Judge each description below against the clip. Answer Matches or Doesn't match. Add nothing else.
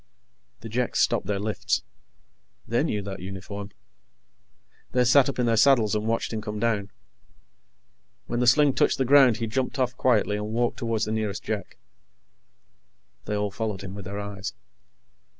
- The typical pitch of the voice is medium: Doesn't match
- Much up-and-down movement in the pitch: Doesn't match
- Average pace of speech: Matches